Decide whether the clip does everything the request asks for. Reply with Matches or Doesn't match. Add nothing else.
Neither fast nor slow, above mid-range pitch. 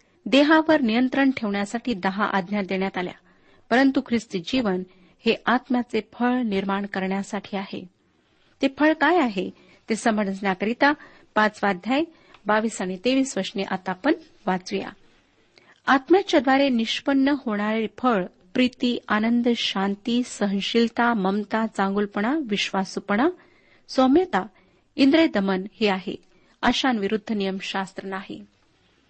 Matches